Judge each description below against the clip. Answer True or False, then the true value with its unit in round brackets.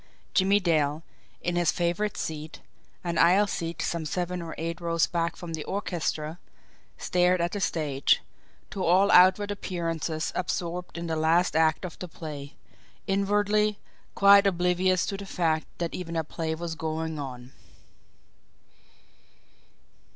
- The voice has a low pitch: False (170 Hz)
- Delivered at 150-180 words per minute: False (140 wpm)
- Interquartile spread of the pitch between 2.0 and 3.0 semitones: True (2.5 semitones)